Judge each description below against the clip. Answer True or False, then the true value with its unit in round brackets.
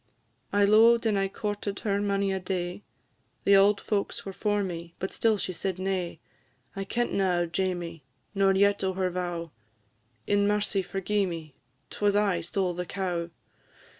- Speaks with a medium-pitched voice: False (195 Hz)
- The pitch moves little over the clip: True (2.2 semitones)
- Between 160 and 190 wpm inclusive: True (165 wpm)